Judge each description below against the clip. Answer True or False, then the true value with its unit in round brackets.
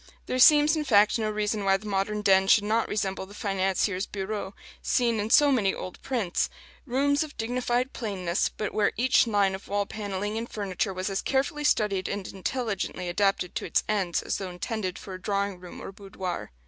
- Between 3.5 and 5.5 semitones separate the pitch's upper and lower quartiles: False (3.0 semitones)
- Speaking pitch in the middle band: False (205 Hz)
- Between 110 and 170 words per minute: False (195 wpm)